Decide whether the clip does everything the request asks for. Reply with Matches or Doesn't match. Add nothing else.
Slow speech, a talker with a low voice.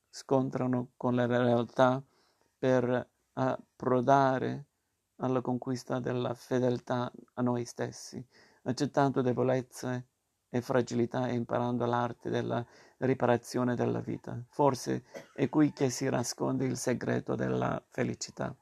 Matches